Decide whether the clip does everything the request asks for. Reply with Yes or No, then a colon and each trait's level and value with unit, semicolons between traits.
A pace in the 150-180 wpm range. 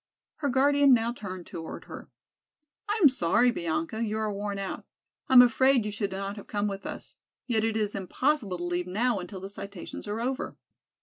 No: average, 195 wpm